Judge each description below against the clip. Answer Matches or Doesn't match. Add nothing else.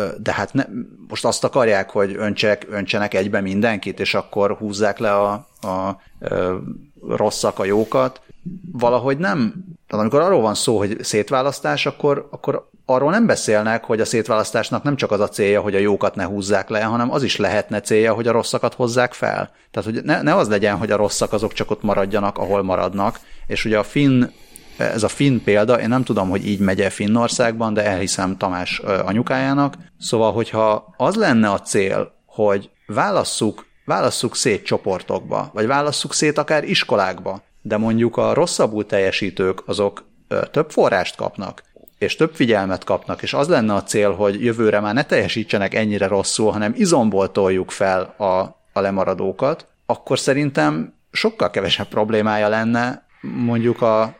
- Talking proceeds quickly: Matches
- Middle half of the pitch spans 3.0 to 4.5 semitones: Matches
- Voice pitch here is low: Matches